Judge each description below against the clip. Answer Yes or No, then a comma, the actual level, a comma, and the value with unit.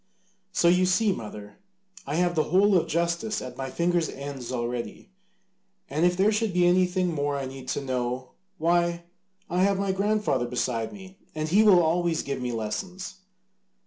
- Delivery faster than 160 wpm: Yes, average, 175 wpm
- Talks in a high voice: No, medium, 170 Hz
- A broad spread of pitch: Yes, wide, 5.8 semitones